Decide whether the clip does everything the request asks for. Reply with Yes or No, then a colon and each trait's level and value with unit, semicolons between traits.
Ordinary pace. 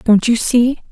Yes: average, 195 wpm